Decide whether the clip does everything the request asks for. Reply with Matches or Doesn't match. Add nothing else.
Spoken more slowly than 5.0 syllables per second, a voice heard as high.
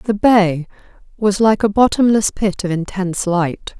Matches